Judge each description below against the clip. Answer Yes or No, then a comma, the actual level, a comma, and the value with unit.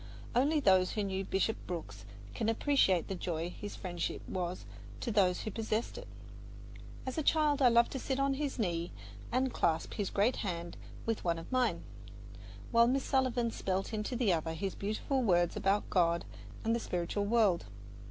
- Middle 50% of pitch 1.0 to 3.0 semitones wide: No, wide, 5.6 semitones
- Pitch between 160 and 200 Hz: No, high, 210 Hz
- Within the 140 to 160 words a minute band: No, average, 175 wpm